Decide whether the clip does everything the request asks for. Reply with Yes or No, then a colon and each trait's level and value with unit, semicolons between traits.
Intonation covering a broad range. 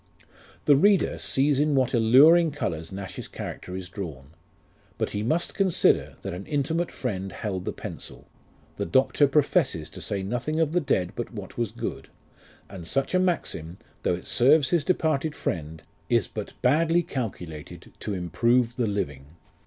Yes: wide, 8.3 semitones